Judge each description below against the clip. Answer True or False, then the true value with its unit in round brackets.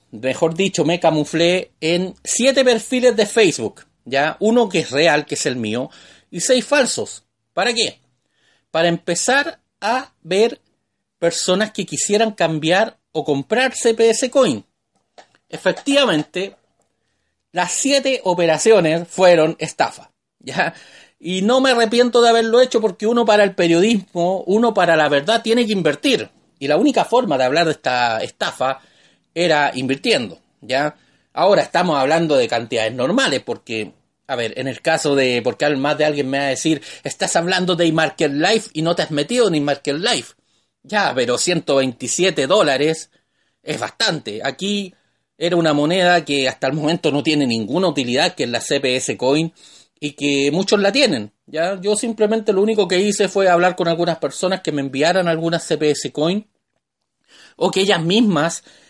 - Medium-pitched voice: True (175 Hz)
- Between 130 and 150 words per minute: False (160 wpm)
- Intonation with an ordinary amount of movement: False (5.9 semitones)